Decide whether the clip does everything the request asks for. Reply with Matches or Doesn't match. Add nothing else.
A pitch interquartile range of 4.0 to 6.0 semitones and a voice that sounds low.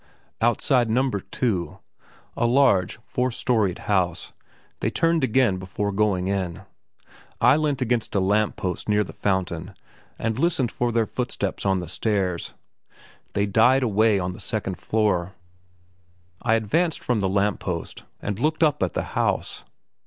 Matches